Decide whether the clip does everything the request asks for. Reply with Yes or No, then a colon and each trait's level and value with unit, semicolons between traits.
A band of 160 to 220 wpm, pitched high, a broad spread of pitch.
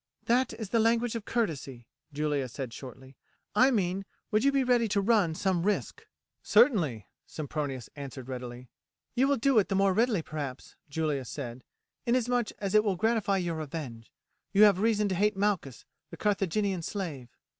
Yes: average, 165 wpm; high, 195 Hz; wide, 7.6 semitones